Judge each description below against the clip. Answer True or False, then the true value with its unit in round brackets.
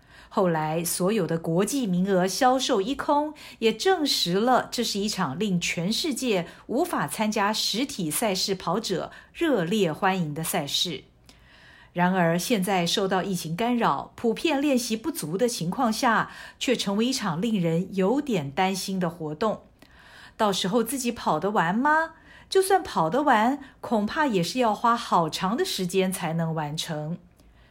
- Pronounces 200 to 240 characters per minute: True (225 characters per minute)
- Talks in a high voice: True (200 Hz)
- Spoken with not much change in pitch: False (5.1 semitones)